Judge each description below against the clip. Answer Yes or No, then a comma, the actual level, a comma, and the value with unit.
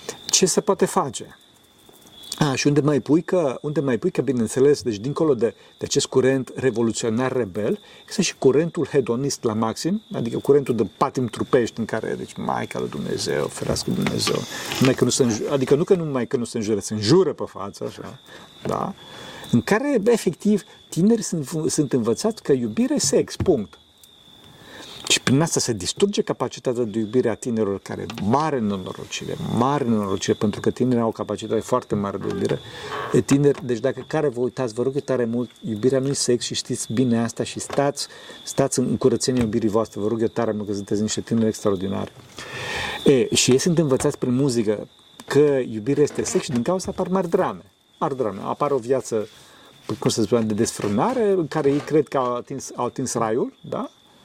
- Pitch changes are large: No, average, 4.7 semitones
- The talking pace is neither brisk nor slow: No, fast, 190 wpm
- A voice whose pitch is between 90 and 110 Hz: No, low, 130 Hz